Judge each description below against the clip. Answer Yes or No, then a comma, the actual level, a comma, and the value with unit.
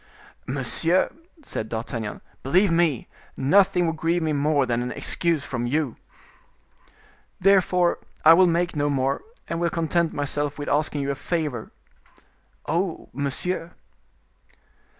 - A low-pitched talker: No, medium, 155 Hz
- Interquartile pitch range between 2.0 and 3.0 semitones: No, average, 3.9 semitones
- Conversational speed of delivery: No, slow, 130 wpm